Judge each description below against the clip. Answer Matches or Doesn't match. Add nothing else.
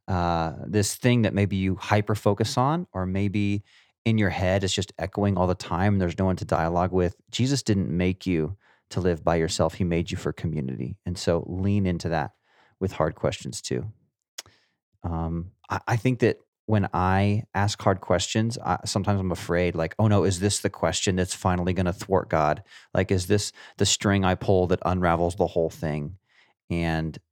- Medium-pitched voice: Doesn't match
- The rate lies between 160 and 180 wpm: Doesn't match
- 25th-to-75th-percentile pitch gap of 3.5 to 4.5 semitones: Doesn't match